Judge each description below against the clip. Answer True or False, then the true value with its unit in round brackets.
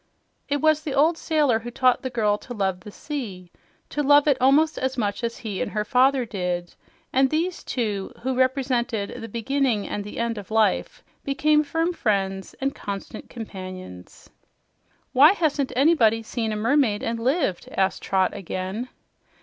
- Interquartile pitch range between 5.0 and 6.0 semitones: True (5.3 semitones)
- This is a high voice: True (240 Hz)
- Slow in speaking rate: False (165 wpm)